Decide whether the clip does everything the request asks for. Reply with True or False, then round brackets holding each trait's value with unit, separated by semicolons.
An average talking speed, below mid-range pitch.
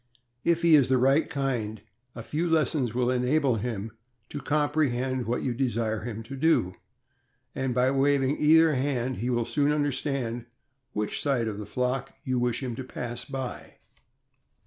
True (165 wpm; 130 Hz)